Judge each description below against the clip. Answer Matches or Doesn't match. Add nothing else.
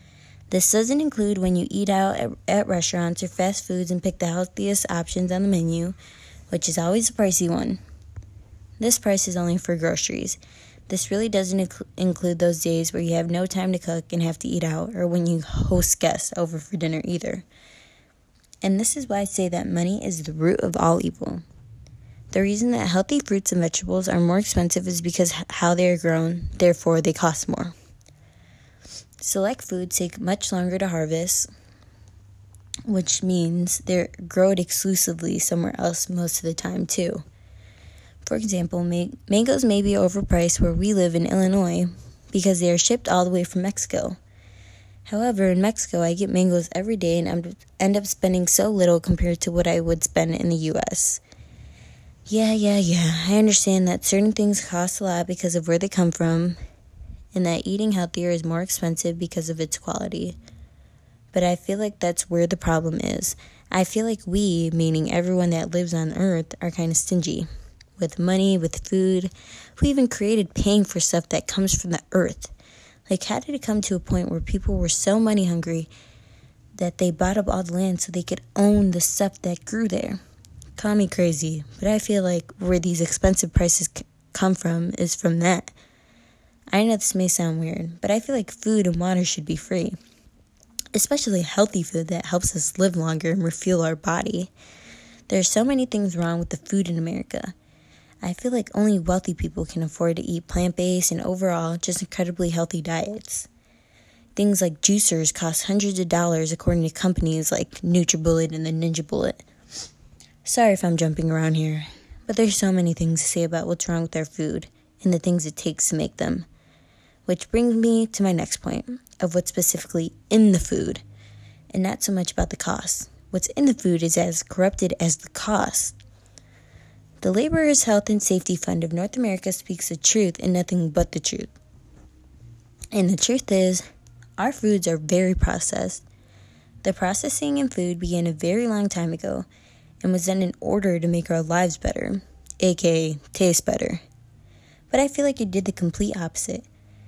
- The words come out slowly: Doesn't match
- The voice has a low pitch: Doesn't match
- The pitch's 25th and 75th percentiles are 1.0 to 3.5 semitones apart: Matches